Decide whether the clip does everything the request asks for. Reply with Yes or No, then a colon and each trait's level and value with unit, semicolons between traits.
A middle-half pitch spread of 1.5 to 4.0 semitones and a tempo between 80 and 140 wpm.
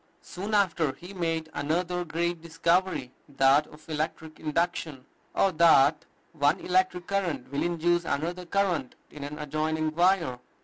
Yes: average, 2.8 semitones; slow, 135 wpm